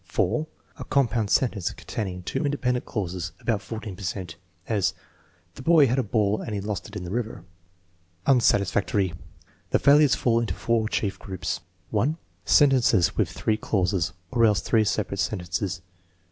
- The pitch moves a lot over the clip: No, average, 4.2 semitones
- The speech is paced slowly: No, average, 160 wpm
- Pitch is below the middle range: Yes, low, 105 Hz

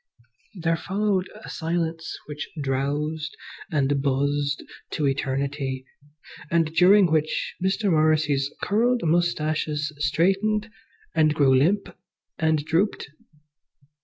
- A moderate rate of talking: No, slow, 100 wpm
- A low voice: No, medium, 155 Hz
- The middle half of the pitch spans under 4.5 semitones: Yes, average, 3.4 semitones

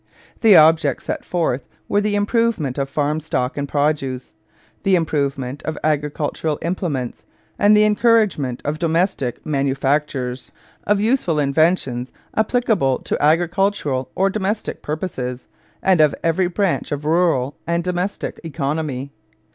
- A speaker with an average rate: No, slow, 125 wpm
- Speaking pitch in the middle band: Yes, medium, 155 Hz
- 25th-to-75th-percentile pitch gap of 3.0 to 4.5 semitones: No, average, 5.3 semitones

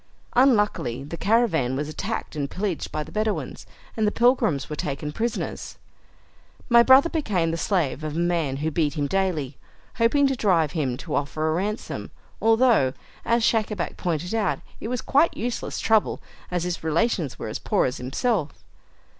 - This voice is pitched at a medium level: Yes, medium, 175 Hz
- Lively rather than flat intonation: Yes, wide, 7.0 semitones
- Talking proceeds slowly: No, average, 170 wpm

